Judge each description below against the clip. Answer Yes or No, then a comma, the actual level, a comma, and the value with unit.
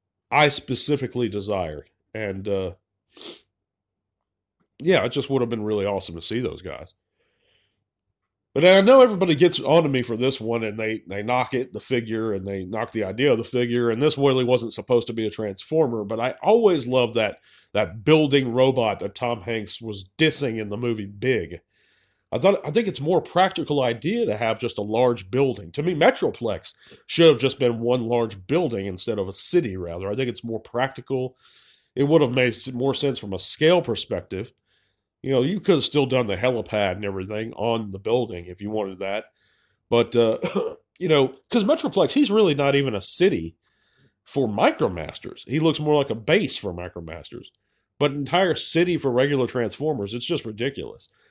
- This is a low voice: Yes, low, 120 Hz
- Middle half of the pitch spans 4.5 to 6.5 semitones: Yes, wide, 5.5 semitones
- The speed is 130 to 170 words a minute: No, average, 190 wpm